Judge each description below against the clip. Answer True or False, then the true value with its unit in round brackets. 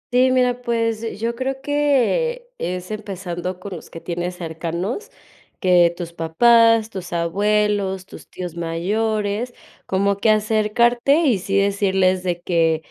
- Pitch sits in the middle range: False (200 Hz)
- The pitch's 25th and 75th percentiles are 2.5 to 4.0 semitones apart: False (4.5 semitones)